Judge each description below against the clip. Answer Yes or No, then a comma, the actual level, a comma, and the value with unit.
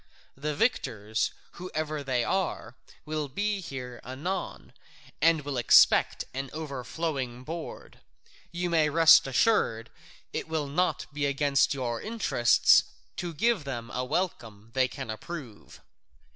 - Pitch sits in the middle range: Yes, medium, 145 Hz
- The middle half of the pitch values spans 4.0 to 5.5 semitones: Yes, average, 4.7 semitones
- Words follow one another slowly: Yes, slow, 125 wpm